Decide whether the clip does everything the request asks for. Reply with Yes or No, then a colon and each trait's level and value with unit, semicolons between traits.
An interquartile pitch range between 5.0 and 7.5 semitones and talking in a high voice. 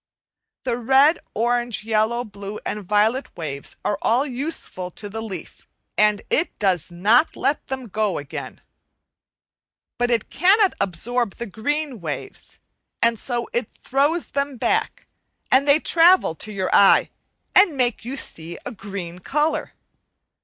Yes: average, 5.3 semitones; high, 235 Hz